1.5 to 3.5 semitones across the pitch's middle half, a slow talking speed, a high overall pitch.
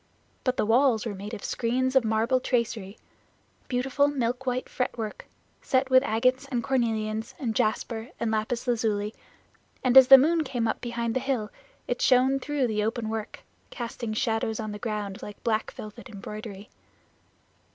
No: average, 3.0 semitones; average, 160 wpm; high, 235 Hz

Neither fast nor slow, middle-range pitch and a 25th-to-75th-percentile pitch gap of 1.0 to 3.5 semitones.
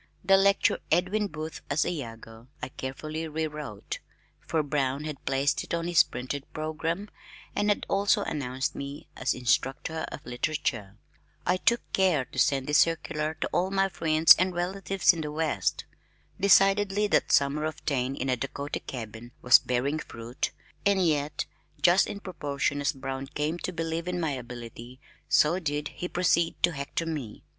No: average, 165 wpm; medium, 155 Hz; average, 4.6 semitones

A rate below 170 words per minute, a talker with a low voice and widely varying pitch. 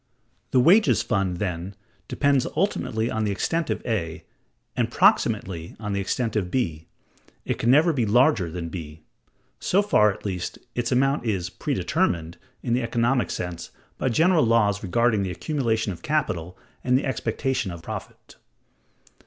Yes: average, 155 wpm; low, 110 Hz; wide, 6.3 semitones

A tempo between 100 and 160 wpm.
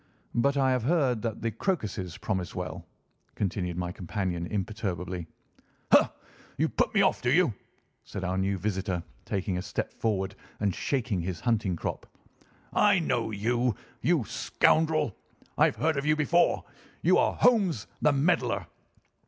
Yes: average, 155 wpm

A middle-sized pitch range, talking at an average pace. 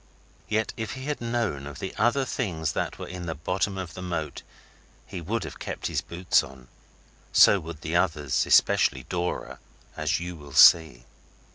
Yes: average, 4.6 semitones; average, 175 wpm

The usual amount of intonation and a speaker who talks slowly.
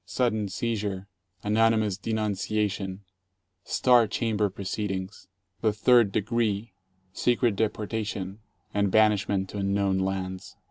No: narrow, 2.2 semitones; slow, 100 wpm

